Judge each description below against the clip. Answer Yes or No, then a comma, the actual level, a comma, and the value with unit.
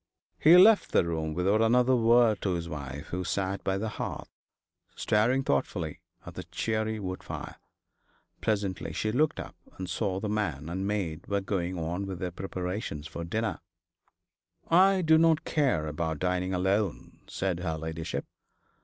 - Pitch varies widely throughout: No, average, 4.5 semitones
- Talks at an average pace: Yes, average, 160 wpm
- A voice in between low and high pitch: No, very low, 95 Hz